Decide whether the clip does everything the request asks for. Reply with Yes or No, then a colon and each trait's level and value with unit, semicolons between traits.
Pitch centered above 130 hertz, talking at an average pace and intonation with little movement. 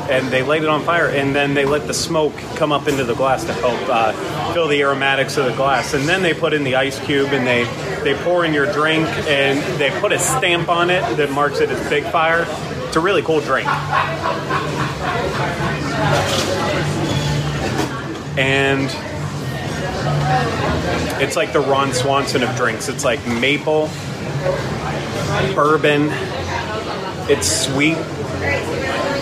Yes: medium, 140 Hz; average, 150 wpm; narrow, 2.1 semitones